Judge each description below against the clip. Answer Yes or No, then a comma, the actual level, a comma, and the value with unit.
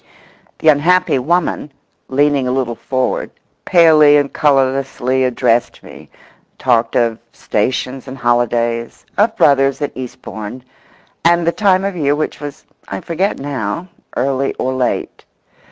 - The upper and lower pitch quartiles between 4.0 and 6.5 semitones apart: No, average, 3.6 semitones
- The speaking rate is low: Yes, slow, 125 wpm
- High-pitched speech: No, low, 135 Hz